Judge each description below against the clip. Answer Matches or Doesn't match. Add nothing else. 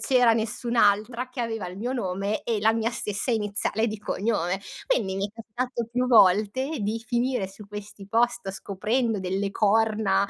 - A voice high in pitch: Matches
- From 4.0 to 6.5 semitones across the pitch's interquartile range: Doesn't match